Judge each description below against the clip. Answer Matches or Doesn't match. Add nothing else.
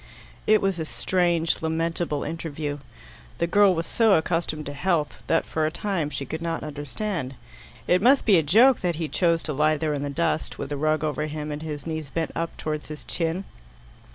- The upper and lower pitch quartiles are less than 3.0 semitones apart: Matches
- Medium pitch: Matches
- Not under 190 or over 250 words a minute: Matches